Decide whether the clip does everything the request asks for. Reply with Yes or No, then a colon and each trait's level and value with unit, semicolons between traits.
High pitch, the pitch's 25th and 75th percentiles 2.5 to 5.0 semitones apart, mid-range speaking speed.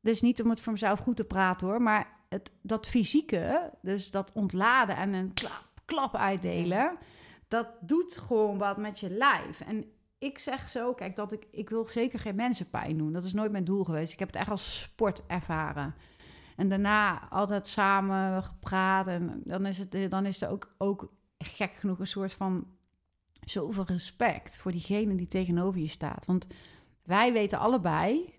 Yes: high, 195 Hz; average, 3.0 semitones; average, 175 wpm